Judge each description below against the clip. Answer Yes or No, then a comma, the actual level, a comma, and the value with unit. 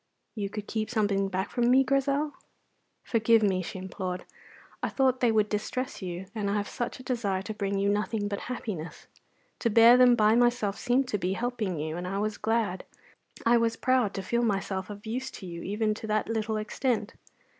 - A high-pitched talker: Yes, high, 215 Hz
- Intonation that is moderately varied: Yes, average, 3.3 semitones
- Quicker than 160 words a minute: Yes, average, 200 wpm